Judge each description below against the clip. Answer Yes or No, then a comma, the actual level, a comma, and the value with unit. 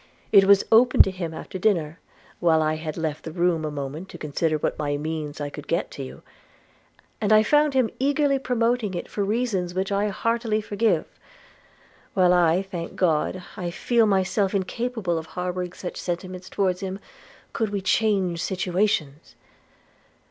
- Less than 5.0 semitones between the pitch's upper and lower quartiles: Yes, average, 4.4 semitones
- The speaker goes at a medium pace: Yes, average, 165 wpm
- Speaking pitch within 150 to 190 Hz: Yes, medium, 185 Hz